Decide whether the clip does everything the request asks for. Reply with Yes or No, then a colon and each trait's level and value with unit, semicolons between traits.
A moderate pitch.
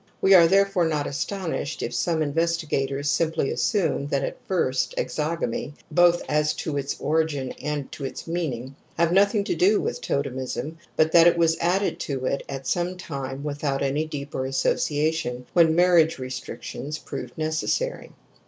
Yes: medium, 155 Hz